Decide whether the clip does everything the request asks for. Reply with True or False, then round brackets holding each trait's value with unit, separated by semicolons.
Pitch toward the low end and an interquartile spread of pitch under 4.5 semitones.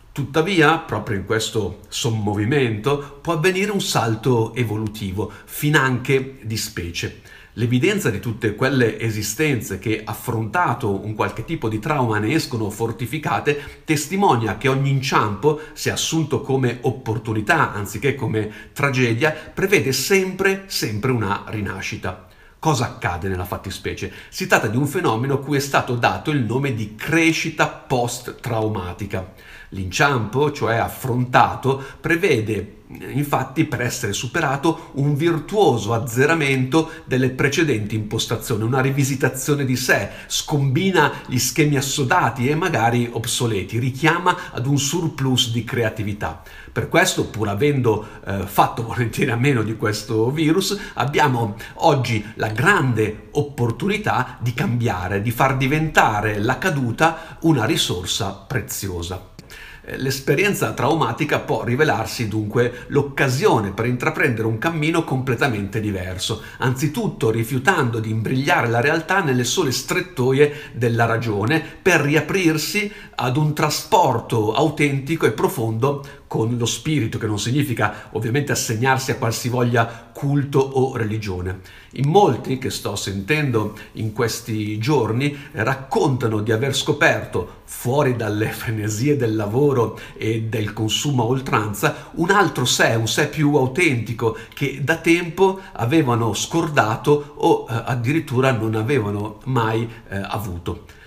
False (125 Hz; 4.8 semitones)